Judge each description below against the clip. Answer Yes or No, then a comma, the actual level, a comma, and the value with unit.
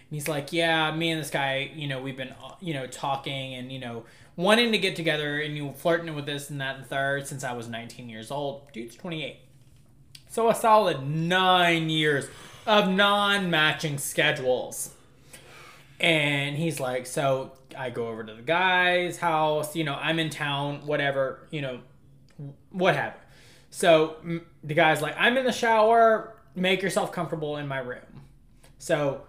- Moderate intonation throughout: Yes, average, 4.0 semitones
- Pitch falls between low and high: Yes, medium, 150 Hz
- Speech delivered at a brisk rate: No, average, 170 wpm